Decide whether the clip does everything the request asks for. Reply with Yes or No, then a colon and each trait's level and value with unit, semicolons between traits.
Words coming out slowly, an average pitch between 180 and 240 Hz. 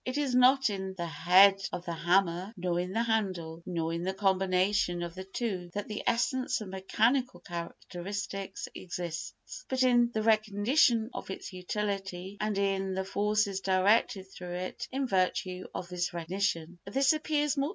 No: average, 155 wpm; high, 190 Hz